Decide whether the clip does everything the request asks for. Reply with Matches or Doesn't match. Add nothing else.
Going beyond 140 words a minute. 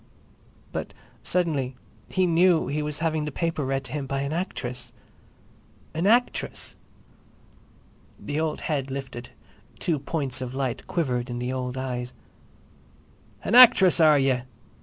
Doesn't match